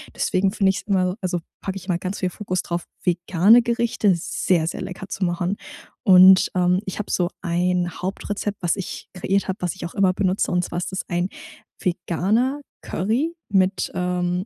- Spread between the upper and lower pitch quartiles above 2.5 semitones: No, narrow, 1.8 semitones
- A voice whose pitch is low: No, medium, 185 Hz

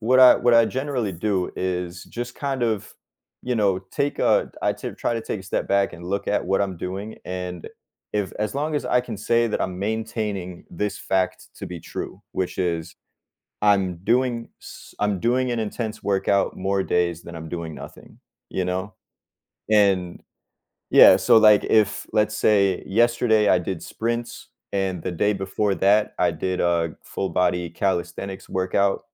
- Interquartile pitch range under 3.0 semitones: No, average, 3.4 semitones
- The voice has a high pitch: No, low, 100 Hz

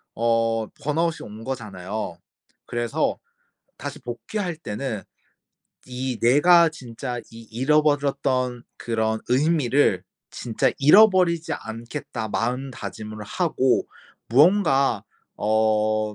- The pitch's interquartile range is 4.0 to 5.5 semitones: Yes, average, 5.1 semitones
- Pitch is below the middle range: Yes, low, 125 Hz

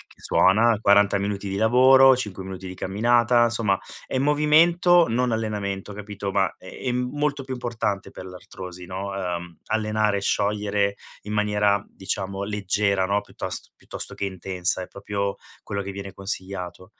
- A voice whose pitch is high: No, low, 100 Hz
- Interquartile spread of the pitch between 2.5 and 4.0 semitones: Yes, average, 2.9 semitones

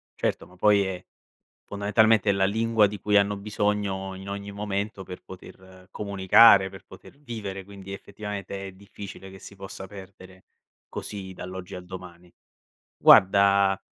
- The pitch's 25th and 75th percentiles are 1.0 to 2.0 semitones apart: Yes, narrow, 1.4 semitones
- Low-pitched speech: Yes, low, 100 Hz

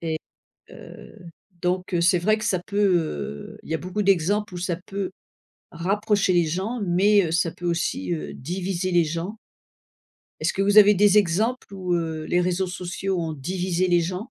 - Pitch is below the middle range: No, medium, 180 Hz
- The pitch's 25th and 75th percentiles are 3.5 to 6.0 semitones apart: No, average, 2.7 semitones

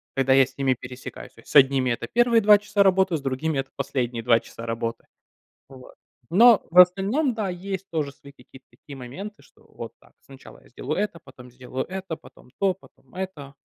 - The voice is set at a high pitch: No, medium, 145 Hz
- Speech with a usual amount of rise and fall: No, wide, 6.8 semitones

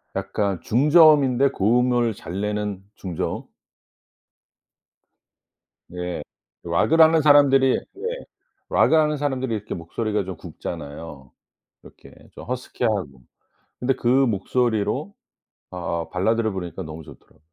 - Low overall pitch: Yes, low, 110 Hz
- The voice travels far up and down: Yes, wide, 6.8 semitones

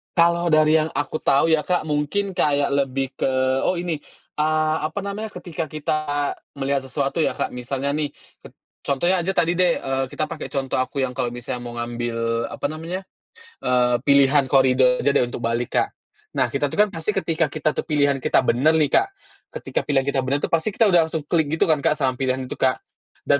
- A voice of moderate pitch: Yes, medium, 145 Hz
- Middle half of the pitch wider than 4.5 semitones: No, average, 3.4 semitones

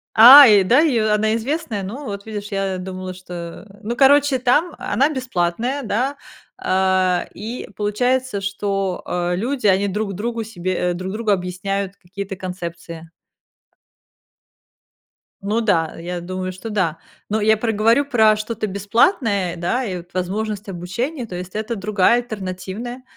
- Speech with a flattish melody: No, average, 4.0 semitones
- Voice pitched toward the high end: Yes, high, 205 Hz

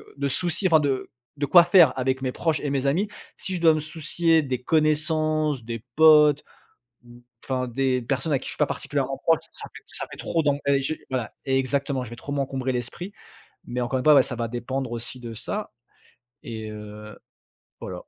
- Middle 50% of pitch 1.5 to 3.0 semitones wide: No, average, 3.7 semitones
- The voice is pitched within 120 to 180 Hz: Yes, low, 135 Hz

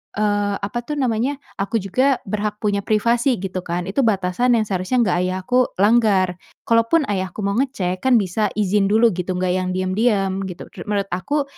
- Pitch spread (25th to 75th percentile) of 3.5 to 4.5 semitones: Yes, average, 3.8 semitones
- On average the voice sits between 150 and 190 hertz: No, high, 205 Hz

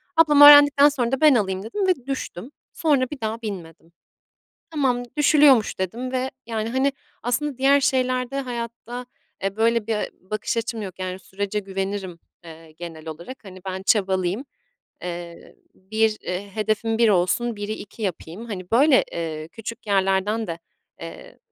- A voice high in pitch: Yes, high, 220 Hz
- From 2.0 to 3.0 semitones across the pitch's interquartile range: No, average, 5.2 semitones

